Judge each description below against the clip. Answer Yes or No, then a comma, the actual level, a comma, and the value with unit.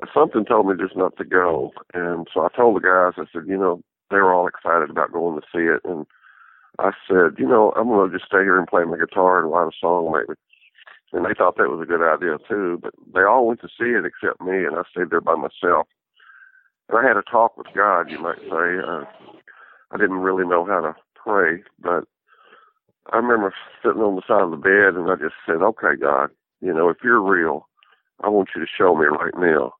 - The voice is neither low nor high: No, very low, 95 Hz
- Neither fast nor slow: No, fast, 235 wpm